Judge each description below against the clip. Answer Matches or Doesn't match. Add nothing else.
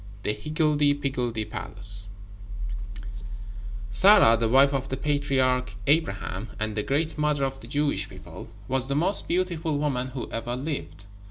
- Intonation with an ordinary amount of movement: Matches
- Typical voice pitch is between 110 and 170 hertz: Matches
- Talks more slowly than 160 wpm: Matches